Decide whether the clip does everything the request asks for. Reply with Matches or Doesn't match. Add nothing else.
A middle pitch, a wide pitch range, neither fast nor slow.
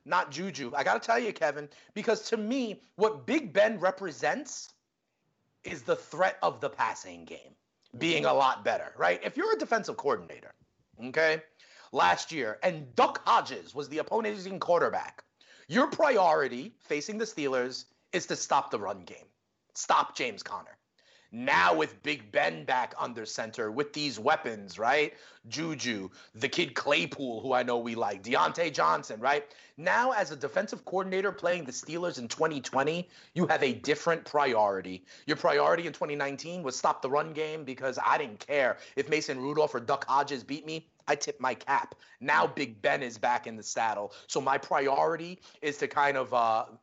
Matches